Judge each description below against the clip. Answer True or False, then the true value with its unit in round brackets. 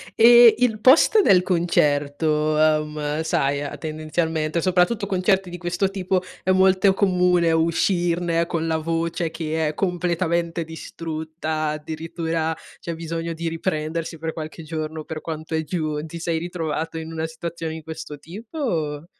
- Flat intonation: True (2.0 semitones)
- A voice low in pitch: False (165 Hz)